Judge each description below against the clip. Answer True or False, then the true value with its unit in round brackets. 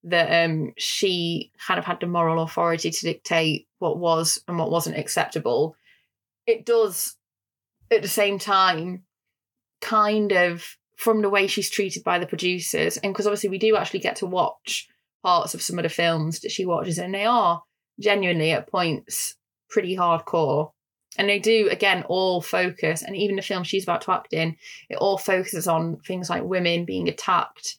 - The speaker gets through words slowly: False (180 wpm)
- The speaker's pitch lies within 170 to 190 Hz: True (185 Hz)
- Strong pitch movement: False (3.4 semitones)